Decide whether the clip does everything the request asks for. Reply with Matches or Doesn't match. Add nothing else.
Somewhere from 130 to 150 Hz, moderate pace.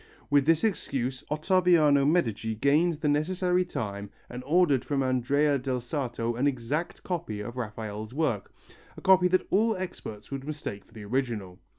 Matches